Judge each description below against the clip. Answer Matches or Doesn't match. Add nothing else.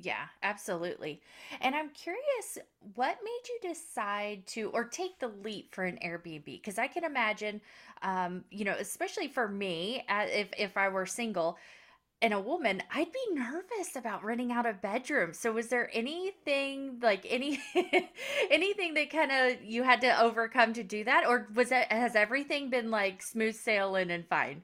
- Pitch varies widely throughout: Matches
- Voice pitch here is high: Matches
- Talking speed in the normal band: Matches